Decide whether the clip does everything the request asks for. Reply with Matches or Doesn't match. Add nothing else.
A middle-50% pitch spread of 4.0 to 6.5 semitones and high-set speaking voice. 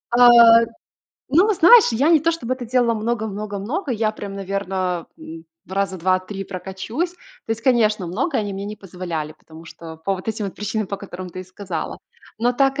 Matches